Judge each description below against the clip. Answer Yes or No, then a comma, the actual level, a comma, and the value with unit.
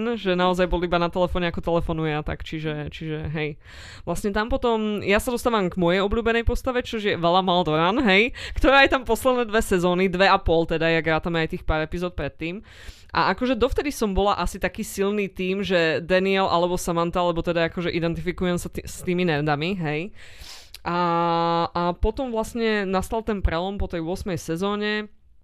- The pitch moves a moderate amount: Yes, average, 3.8 semitones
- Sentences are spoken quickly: Yes, fast, 185 wpm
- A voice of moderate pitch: Yes, medium, 180 Hz